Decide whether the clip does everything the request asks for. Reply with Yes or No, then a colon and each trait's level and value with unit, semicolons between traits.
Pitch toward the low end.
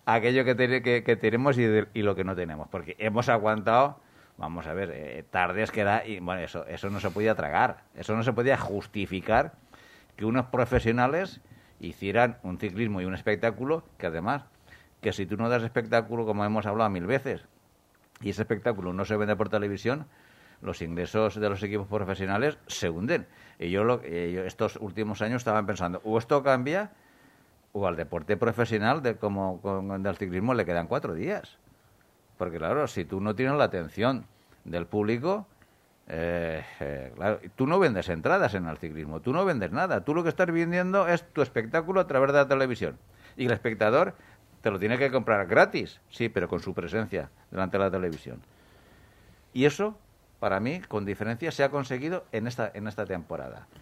Yes: low, 110 Hz